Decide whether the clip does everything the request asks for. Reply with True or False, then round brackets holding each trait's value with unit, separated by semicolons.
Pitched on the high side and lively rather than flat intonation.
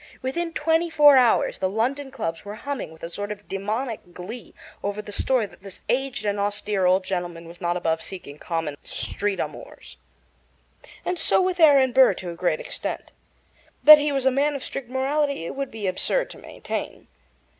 True (220 Hz; 6.8 semitones)